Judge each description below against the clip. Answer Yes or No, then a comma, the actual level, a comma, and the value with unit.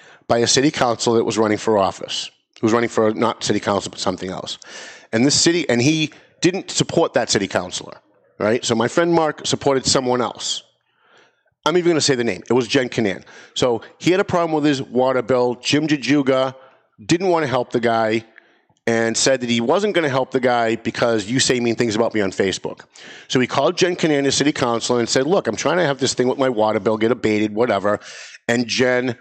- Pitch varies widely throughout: No, average, 3.4 semitones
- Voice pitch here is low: Yes, low, 125 Hz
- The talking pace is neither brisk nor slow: No, fast, 225 wpm